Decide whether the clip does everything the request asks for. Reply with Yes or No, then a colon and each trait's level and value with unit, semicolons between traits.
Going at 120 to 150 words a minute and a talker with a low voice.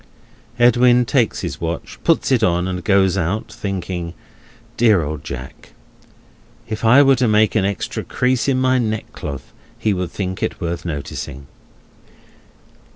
Yes: average, 145 wpm; low, 100 Hz